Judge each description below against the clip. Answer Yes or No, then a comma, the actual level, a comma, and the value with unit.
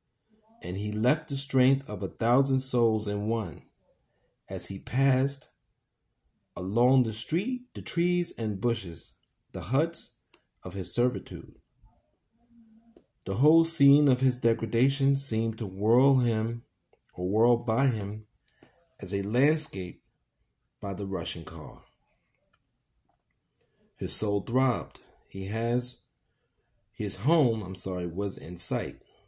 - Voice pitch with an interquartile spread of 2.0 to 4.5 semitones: No, average, 5.3 semitones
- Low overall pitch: Yes, low, 115 Hz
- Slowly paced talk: Yes, slow, 120 wpm